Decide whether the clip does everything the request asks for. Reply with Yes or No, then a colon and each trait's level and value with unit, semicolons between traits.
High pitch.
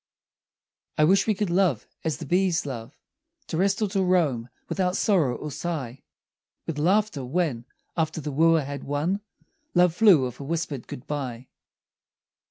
No: medium, 160 Hz